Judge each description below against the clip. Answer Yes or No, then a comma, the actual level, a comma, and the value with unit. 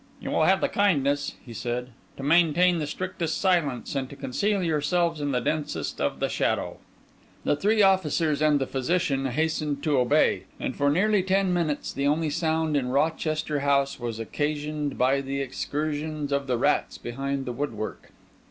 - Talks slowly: No, average, 170 wpm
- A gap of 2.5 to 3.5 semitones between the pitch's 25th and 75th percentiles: Yes, average, 2.9 semitones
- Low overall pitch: No, medium, 145 Hz